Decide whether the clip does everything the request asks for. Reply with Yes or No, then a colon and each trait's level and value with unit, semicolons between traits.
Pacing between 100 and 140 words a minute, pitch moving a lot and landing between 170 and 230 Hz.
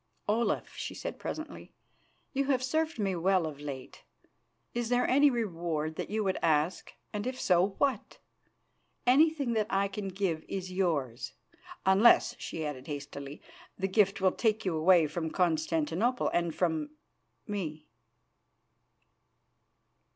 Yes: slow, 135 wpm; wide, 6.0 semitones; high, 190 Hz